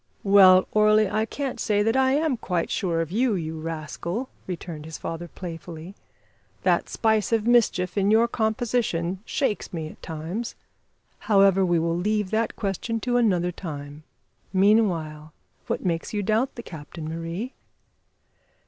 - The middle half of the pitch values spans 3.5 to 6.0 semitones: Yes, average, 4.9 semitones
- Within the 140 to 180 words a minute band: Yes, average, 150 wpm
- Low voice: No, high, 190 Hz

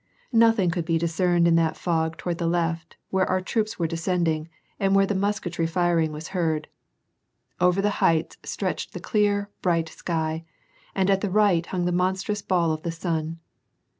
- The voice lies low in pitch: No, medium, 175 Hz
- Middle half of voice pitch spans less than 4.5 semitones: Yes, average, 2.7 semitones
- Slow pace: No, average, 175 wpm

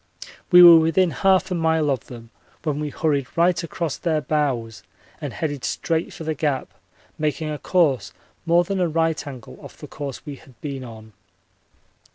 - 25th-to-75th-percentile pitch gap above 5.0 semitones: No, average, 3.3 semitones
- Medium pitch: Yes, medium, 155 Hz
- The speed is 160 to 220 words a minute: Yes, average, 180 wpm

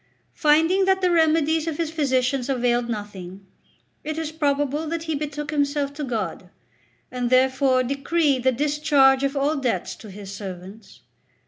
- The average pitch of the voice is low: No, very high, 280 Hz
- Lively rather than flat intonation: No, average, 3.9 semitones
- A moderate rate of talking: Yes, average, 150 wpm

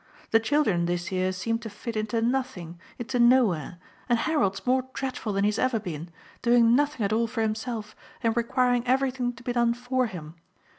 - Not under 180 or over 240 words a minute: Yes, average, 190 wpm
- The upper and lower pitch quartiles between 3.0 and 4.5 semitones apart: Yes, average, 3.6 semitones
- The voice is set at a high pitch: Yes, high, 230 Hz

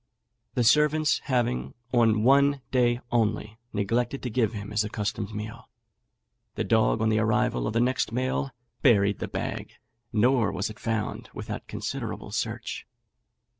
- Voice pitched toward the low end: Yes, low, 115 Hz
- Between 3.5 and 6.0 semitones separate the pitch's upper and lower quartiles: No, average, 3.0 semitones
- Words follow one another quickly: No, average, 145 wpm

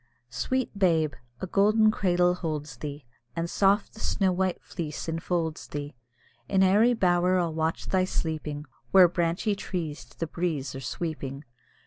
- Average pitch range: Yes, average, 3.6 semitones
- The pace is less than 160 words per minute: Yes, average, 150 wpm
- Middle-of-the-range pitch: Yes, medium, 170 Hz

